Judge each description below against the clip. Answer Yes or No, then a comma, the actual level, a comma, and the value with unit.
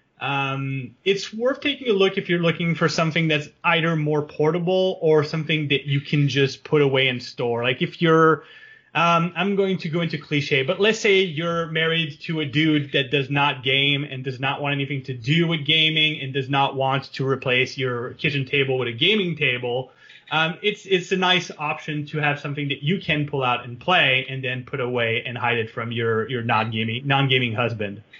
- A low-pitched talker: No, medium, 145 Hz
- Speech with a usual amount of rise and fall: Yes, average, 3.9 semitones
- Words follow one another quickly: Yes, fast, 210 wpm